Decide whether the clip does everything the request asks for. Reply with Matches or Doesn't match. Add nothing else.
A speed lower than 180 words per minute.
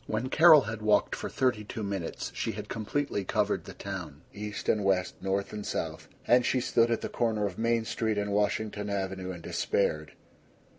Doesn't match